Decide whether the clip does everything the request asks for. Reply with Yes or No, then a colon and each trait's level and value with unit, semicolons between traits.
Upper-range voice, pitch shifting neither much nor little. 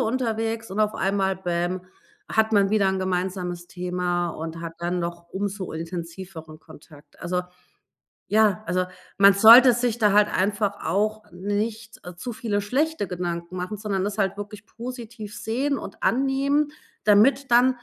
Yes: high, 200 Hz; average, 3.8 semitones